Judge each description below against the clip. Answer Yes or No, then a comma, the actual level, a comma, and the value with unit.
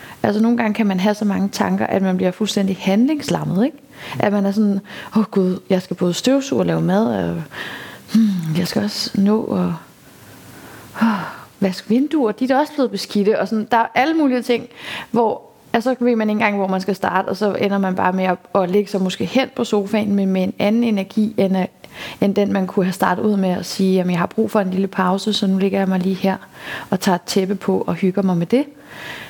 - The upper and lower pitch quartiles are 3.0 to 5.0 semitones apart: No, narrow, 2.6 semitones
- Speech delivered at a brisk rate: Yes, fast, 235 wpm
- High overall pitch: Yes, high, 200 Hz